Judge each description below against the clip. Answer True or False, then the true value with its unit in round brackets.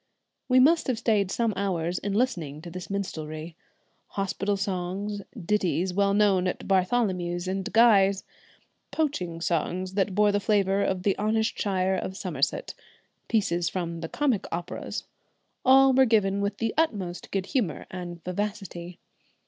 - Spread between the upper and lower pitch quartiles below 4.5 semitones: True (2.9 semitones)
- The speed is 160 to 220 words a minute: False (145 wpm)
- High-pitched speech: True (195 Hz)